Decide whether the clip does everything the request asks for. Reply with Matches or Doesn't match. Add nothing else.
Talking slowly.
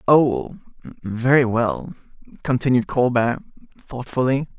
Matches